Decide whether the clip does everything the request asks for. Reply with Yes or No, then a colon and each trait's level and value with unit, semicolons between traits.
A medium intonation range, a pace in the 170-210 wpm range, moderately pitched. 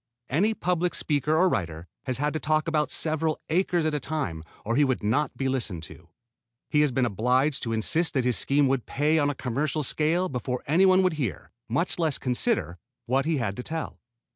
Yes: average, 4.2 semitones; fast, 205 wpm; medium, 145 Hz